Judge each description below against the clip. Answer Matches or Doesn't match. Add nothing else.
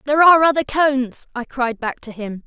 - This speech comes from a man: Doesn't match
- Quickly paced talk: Matches